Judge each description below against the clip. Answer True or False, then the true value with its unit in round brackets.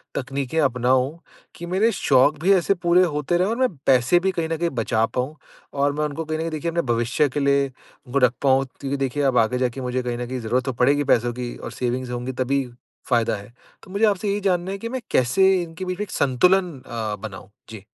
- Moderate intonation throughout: False (5.7 semitones)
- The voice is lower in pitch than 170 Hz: True (140 Hz)